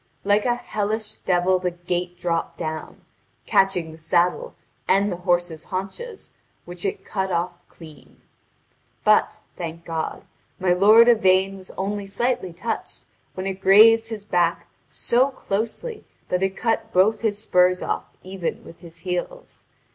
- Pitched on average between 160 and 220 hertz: Yes, high, 190 Hz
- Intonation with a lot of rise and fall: No, average, 3.1 semitones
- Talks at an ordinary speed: Yes, average, 145 wpm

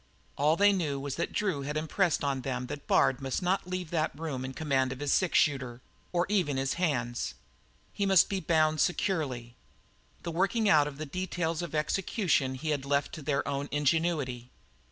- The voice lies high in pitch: No, medium, 150 Hz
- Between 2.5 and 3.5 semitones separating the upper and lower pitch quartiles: No, average, 4.3 semitones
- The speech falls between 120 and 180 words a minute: No, average, 195 wpm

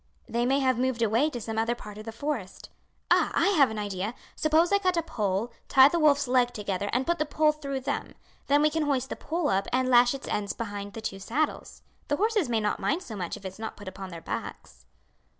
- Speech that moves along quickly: Yes, fast, 240 wpm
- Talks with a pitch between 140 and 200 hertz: No, high, 245 Hz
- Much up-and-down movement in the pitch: Yes, wide, 5.9 semitones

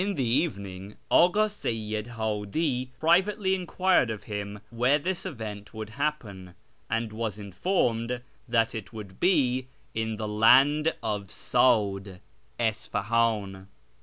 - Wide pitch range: Yes, wide, 5.8 semitones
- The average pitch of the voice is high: No, low, 115 Hz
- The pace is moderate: No, slow, 125 wpm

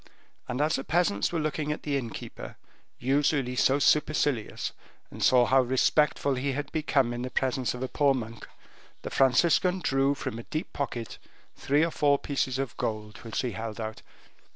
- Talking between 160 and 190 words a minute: Yes, average, 175 wpm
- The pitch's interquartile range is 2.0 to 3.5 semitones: Yes, average, 3.2 semitones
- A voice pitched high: No, low, 135 Hz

